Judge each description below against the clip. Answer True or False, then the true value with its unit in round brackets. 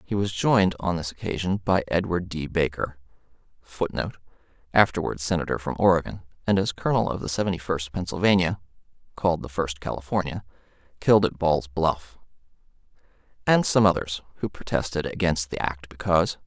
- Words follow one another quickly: False (145 wpm)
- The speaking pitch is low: True (85 Hz)